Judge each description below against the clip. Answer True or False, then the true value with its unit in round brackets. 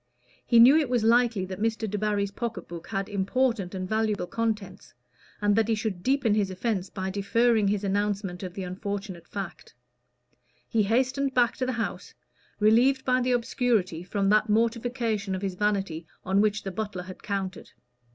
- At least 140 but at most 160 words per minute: False (170 wpm)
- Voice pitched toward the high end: True (210 Hz)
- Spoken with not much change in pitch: False (3.2 semitones)